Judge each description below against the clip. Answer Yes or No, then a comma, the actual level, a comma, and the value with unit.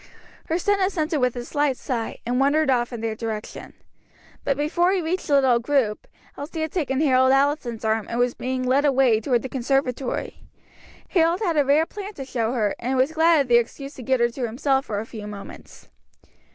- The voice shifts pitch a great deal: No, average, 4.0 semitones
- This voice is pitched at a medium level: No, very high, 265 Hz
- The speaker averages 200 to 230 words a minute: Yes, fast, 205 wpm